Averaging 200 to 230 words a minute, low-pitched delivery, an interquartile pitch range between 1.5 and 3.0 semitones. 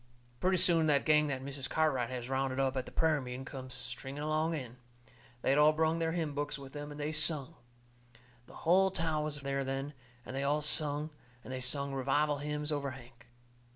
No: fast, 205 wpm; medium, 145 Hz; narrow, 2.5 semitones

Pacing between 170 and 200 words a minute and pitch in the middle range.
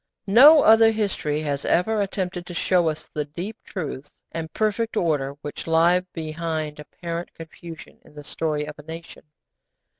No: average, 155 wpm; medium, 165 Hz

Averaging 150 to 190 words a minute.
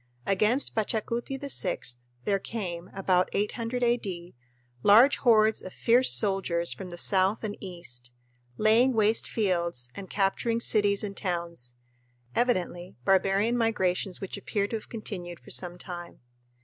No: slow, 135 wpm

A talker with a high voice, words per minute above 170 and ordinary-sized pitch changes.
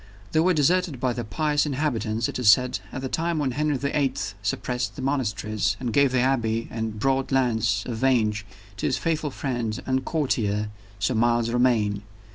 No: low, 125 Hz; average, 190 wpm; average, 3.9 semitones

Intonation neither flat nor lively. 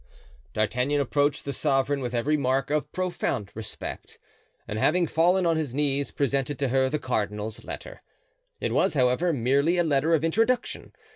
Yes: average, 3.9 semitones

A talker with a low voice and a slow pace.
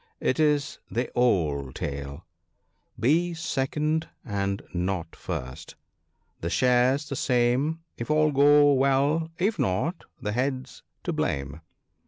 Yes: low, 130 Hz; slow, 130 wpm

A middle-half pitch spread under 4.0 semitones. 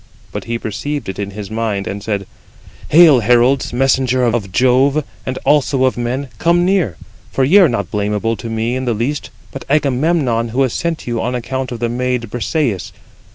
Yes: average, 3.2 semitones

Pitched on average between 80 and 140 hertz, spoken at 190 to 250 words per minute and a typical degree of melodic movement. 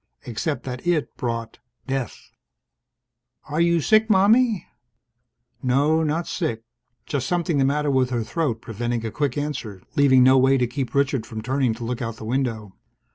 No: low, 135 Hz; average, 165 wpm; average, 4.2 semitones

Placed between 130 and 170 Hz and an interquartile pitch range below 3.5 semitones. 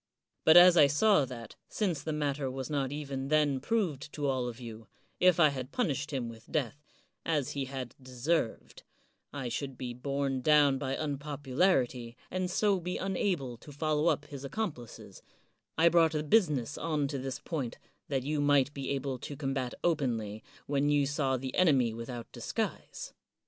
Yes: medium, 140 Hz; average, 3.0 semitones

